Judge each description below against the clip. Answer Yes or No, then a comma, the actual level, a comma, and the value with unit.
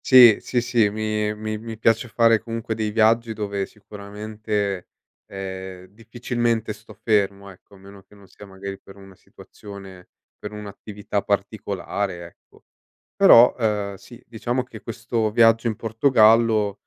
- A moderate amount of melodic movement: No, narrow, 2.3 semitones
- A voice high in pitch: No, low, 105 Hz